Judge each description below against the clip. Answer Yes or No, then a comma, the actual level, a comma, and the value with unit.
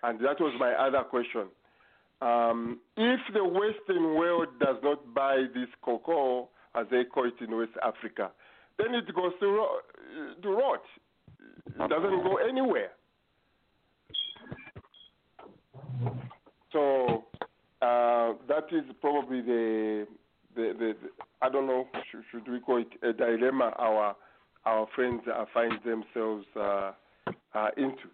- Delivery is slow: Yes, slow, 130 wpm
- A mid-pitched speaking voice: No, low, 125 Hz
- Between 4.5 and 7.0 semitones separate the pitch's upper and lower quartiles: Yes, average, 5.3 semitones